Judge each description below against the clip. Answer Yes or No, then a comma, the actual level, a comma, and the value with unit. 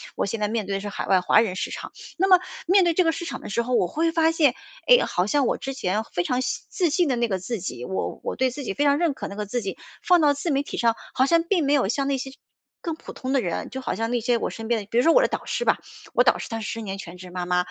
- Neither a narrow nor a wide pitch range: No, wide, 7.4 semitones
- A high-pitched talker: Yes, very high, 250 Hz